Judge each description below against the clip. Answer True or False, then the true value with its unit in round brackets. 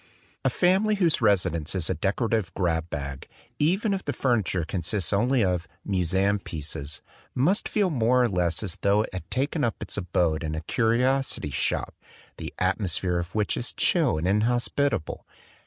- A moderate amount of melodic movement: False (6.5 semitones)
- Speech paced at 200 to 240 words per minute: False (170 wpm)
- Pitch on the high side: False (100 Hz)